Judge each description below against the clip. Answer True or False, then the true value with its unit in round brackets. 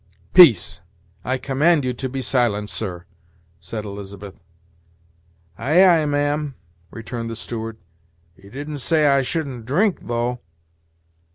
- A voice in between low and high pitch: False (125 Hz)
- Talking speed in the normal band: False (120 wpm)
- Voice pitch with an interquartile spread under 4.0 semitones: False (4.7 semitones)